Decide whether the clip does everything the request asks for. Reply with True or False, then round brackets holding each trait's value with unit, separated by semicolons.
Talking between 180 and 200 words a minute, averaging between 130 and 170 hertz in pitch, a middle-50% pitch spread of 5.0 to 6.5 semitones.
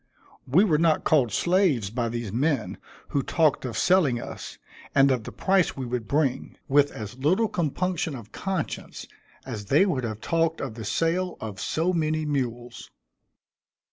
False (165 wpm; 140 Hz; 5.6 semitones)